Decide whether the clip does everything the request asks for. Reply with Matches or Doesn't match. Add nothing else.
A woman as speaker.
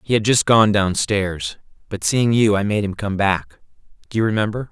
Doesn't match